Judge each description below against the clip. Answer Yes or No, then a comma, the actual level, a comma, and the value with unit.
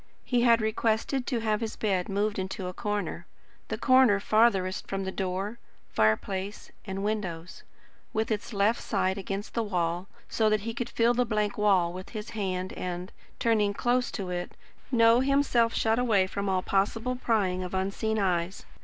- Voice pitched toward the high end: Yes, high, 205 Hz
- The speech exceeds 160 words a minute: Yes, average, 170 wpm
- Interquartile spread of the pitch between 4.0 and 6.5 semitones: No, average, 3.3 semitones